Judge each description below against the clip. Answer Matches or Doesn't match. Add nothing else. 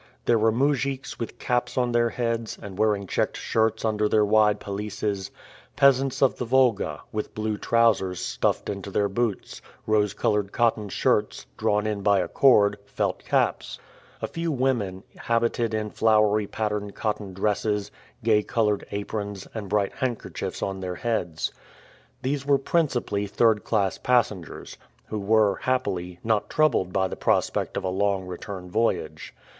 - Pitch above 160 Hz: Doesn't match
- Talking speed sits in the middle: Matches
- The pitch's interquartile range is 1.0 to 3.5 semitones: Matches